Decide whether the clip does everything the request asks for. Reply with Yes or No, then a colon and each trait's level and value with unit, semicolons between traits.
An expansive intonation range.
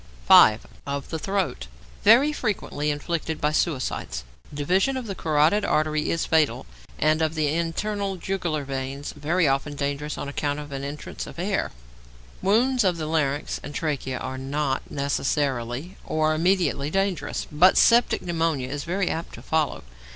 No: average, 4.2 semitones